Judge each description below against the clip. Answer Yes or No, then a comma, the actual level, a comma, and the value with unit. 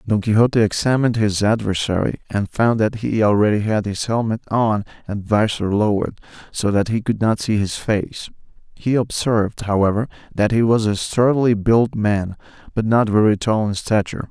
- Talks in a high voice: No, low, 110 Hz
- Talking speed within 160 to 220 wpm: Yes, average, 170 wpm